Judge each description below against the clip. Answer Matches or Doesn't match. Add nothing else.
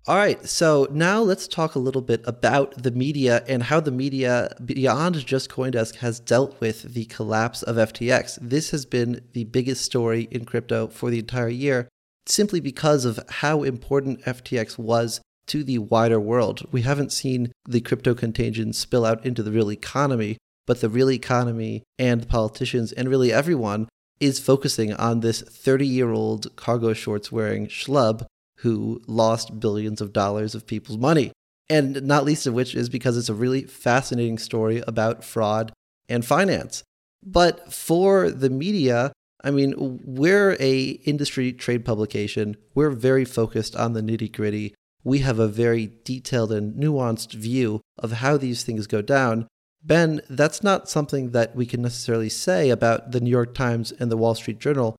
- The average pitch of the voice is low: Matches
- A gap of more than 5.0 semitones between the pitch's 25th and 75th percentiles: Doesn't match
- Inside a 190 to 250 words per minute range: Doesn't match